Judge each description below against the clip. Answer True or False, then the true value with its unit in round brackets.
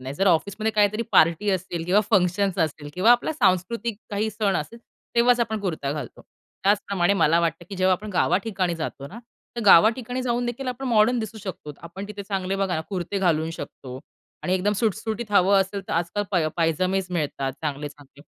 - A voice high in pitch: True (195 Hz)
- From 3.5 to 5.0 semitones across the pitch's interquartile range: True (4.1 semitones)